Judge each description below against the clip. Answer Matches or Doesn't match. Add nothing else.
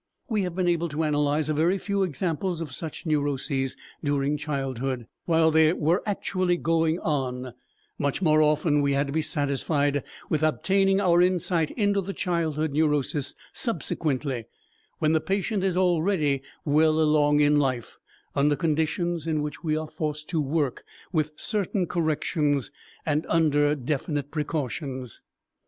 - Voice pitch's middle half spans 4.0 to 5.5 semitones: Doesn't match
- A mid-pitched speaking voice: Matches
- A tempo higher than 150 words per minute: Doesn't match